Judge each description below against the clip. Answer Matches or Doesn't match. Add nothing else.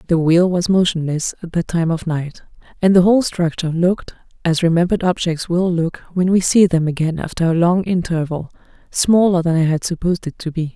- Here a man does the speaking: Doesn't match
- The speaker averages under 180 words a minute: Doesn't match